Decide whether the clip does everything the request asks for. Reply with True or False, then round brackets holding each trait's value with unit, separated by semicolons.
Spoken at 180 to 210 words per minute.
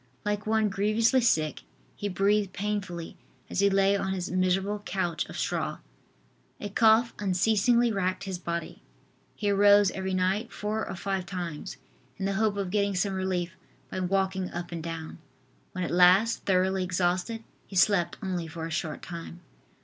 False (165 wpm)